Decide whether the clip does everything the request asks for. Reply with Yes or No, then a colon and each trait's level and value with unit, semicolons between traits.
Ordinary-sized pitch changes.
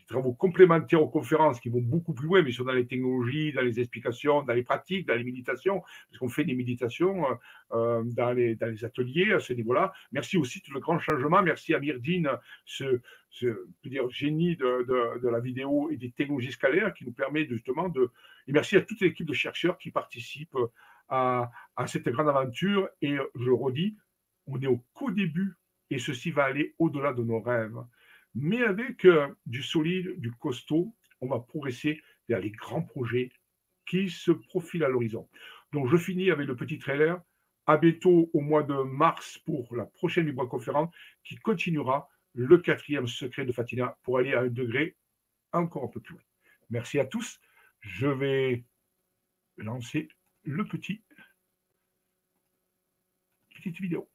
No: wide, 5.7 semitones